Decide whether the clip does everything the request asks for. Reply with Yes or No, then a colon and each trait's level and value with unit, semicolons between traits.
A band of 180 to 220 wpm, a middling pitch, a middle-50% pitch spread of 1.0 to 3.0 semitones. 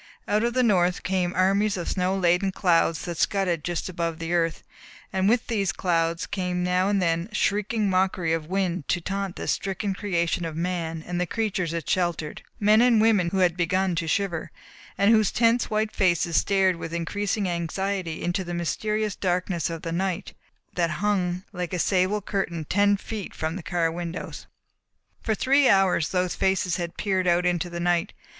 Yes: average, 185 wpm; medium, 180 Hz; narrow, 2.6 semitones